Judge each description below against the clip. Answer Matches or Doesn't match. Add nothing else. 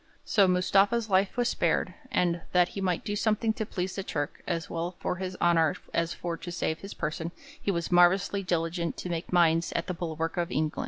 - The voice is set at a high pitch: Doesn't match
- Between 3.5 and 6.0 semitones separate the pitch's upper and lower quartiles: Doesn't match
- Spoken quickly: Matches